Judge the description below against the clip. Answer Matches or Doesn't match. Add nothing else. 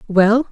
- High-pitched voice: Matches